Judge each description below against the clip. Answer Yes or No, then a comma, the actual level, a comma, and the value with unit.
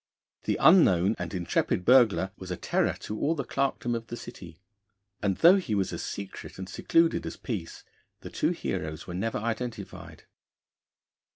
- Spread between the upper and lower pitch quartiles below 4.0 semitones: No, average, 5.2 semitones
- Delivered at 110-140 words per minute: No, average, 165 wpm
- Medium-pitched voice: No, low, 105 Hz